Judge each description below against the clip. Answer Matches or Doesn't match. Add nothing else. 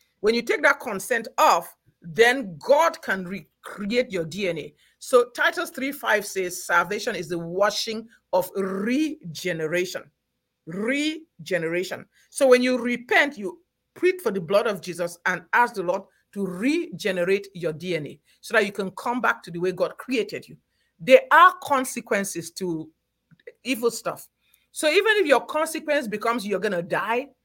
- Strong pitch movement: Matches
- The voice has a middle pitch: Doesn't match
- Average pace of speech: Matches